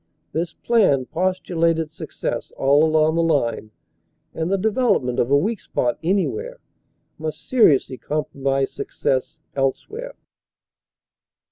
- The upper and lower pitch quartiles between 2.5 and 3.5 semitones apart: No, wide, 5.6 semitones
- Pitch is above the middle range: No, medium, 160 Hz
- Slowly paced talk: Yes, slow, 115 wpm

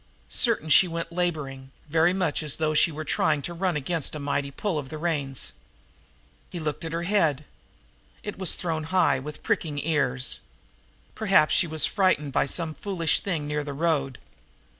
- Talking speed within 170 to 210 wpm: Yes, average, 175 wpm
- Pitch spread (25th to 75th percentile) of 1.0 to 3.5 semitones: Yes, average, 2.9 semitones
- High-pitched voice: No, medium, 155 Hz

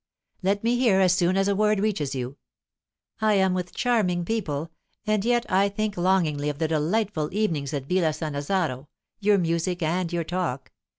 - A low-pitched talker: No, medium, 180 Hz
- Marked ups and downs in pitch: No, average, 4.5 semitones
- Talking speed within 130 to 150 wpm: No, average, 175 wpm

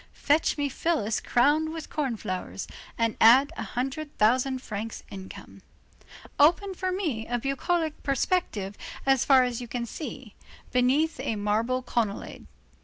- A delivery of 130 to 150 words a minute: Yes, average, 140 wpm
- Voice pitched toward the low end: No, very high, 255 Hz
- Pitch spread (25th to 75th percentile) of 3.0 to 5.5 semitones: Yes, average, 5.1 semitones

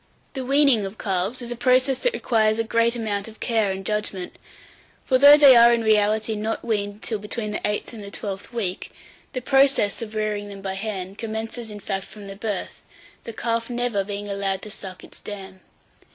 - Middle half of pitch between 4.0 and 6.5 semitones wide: No, average, 2.7 semitones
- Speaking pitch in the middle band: No, high, 215 Hz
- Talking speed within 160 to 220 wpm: Yes, fast, 205 wpm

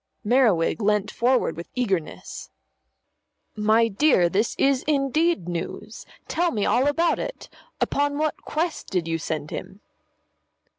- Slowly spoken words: Yes, slow, 130 wpm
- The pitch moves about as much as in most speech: No, wide, 7.2 semitones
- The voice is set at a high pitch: Yes, high, 230 Hz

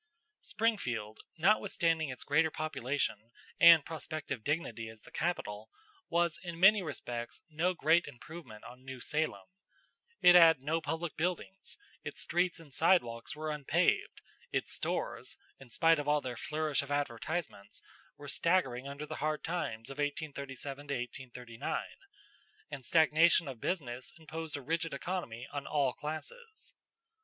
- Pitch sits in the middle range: Yes, medium, 150 Hz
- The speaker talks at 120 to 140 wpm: Yes, slow, 135 wpm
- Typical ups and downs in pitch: Yes, average, 4.3 semitones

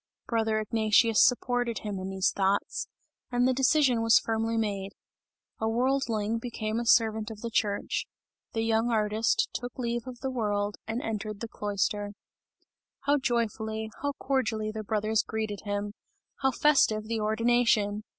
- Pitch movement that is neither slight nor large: No, narrow, 2.1 semitones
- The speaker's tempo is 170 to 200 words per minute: No, average, 150 wpm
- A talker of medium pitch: No, high, 220 Hz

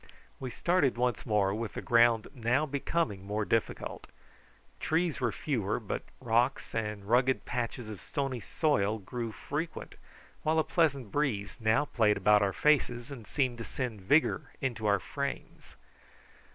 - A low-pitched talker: Yes, low, 120 Hz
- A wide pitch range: No, average, 4.6 semitones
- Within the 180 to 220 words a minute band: No, average, 150 wpm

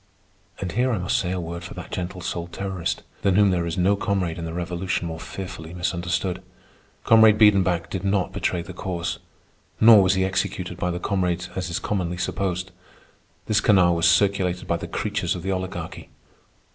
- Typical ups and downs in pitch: No, narrow, 1.9 semitones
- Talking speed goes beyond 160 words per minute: Yes, average, 185 wpm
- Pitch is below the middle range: Yes, very low, 90 Hz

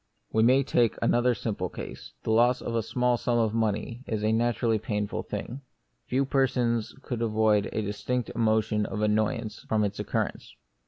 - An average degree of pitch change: No, narrow, 2.1 semitones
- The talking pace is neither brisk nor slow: Yes, average, 170 wpm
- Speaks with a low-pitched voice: Yes, low, 115 Hz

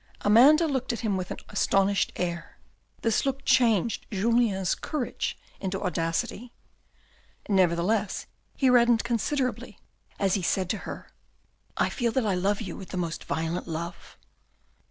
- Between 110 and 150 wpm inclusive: Yes, average, 145 wpm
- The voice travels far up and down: No, average, 4.8 semitones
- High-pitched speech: Yes, high, 205 Hz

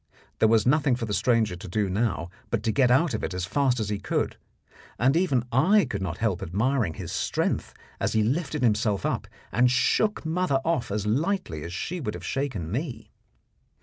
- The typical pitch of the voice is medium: No, low, 115 Hz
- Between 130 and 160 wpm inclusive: No, average, 200 wpm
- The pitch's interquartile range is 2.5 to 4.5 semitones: No, average, 5.3 semitones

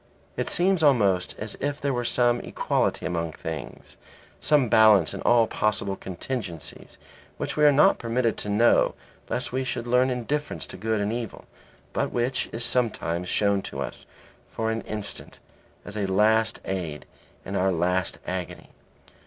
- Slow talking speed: No, average, 160 wpm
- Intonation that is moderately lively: Yes, average, 4.4 semitones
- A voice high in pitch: No, low, 110 Hz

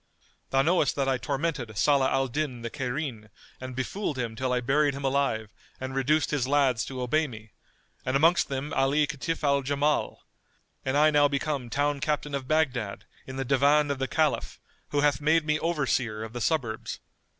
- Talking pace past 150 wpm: Yes, average, 195 wpm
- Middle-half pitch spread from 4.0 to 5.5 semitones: No, average, 2.7 semitones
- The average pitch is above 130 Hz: Yes, medium, 140 Hz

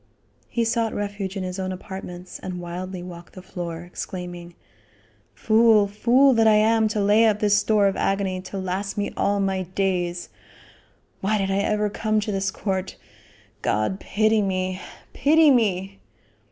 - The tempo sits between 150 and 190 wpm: Yes, average, 160 wpm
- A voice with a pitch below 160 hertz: No, high, 195 Hz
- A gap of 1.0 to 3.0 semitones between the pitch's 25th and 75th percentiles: Yes, narrow, 2.5 semitones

